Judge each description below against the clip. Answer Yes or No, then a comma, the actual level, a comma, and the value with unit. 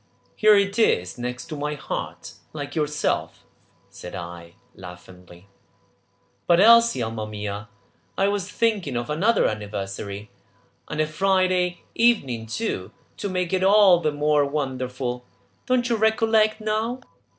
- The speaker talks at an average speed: No, slow, 130 wpm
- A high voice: No, medium, 150 Hz